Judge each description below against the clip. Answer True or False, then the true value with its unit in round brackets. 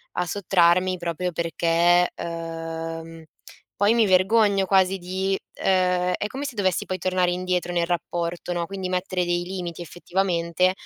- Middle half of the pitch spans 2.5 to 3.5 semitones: False (1.7 semitones)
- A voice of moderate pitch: True (180 Hz)